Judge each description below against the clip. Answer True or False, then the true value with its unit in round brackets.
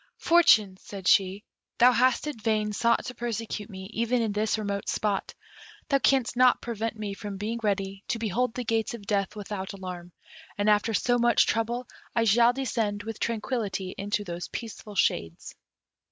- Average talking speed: True (170 wpm)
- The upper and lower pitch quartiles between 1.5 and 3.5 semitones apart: True (2.8 semitones)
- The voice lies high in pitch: True (215 Hz)